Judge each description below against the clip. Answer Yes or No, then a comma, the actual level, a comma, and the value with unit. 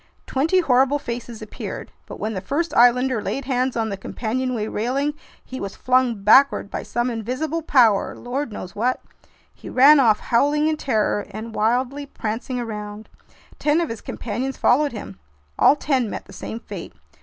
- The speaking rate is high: No, average, 165 wpm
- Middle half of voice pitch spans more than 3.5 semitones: Yes, average, 3.9 semitones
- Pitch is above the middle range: Yes, very high, 250 Hz